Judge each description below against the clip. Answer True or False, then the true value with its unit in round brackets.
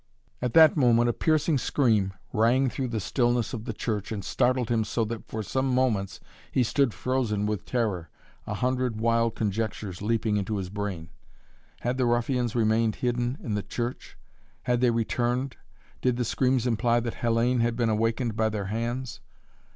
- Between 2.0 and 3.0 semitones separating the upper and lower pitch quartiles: True (2.5 semitones)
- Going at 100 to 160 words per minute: False (175 wpm)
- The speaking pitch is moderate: False (115 Hz)